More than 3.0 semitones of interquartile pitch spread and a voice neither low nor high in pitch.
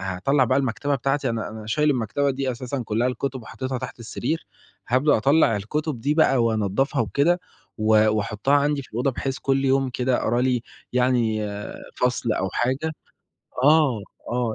No: average, 3.4 semitones; low, 130 Hz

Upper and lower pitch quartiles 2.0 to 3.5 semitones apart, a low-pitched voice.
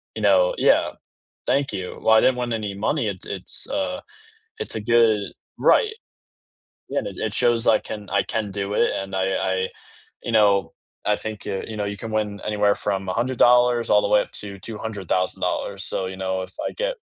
Yes: average, 3.1 semitones; low, 105 Hz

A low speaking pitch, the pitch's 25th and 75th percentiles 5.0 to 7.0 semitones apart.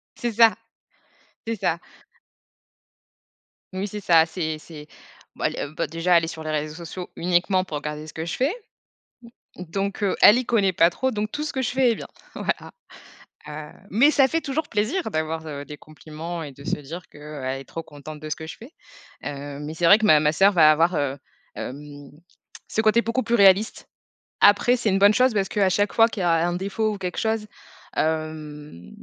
No: medium, 175 Hz; wide, 5.6 semitones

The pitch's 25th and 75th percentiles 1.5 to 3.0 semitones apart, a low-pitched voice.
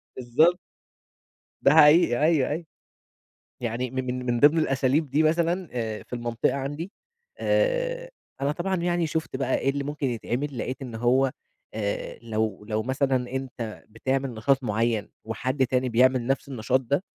No: average, 3.8 semitones; low, 130 Hz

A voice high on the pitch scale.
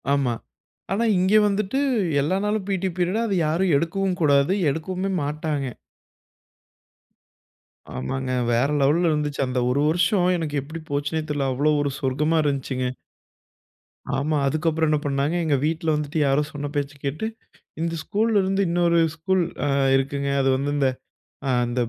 No: medium, 155 Hz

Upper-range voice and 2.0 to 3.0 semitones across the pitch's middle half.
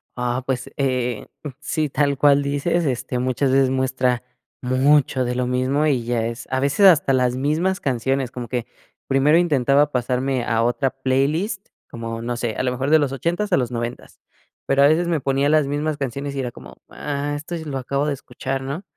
No: low, 135 Hz; narrow, 2.6 semitones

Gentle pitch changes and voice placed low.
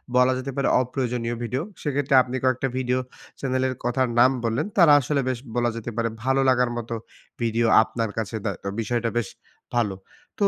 Yes: narrow, 2.0 semitones; low, 125 Hz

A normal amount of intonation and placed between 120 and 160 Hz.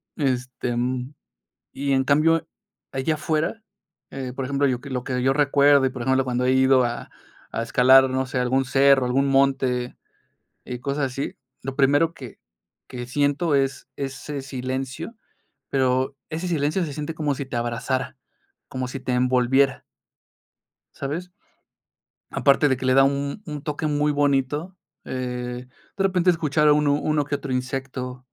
No: narrow, 2.2 semitones; low, 135 Hz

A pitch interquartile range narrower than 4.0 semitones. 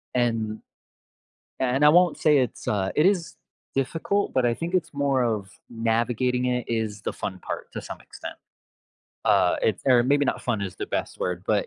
No: average, 4.3 semitones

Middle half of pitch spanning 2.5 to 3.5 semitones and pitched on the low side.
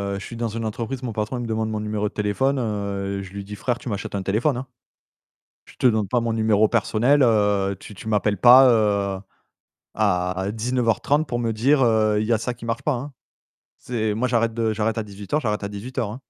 Yes: average, 2.8 semitones; low, 110 Hz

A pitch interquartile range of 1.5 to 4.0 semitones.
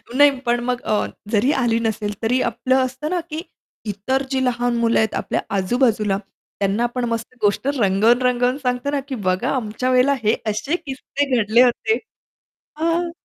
Yes: average, 3.3 semitones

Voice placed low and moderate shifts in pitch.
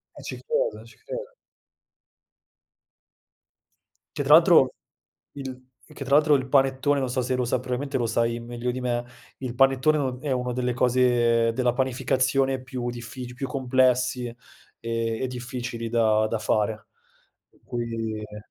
No: low, 125 Hz; narrow, 2.0 semitones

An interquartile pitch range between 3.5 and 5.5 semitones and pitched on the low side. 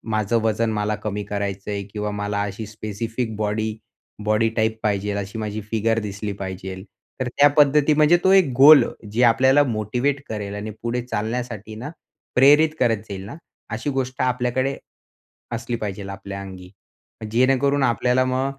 Yes: average, 3.8 semitones; low, 110 Hz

